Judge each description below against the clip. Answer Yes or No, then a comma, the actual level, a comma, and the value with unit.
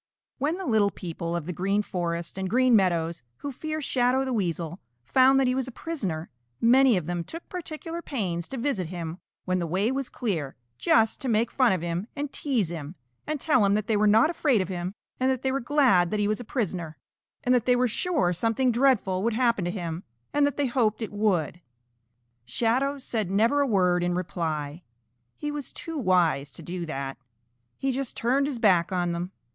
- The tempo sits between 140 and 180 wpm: No, fast, 205 wpm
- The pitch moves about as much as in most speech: No, wide, 6.9 semitones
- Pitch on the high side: Yes, high, 215 Hz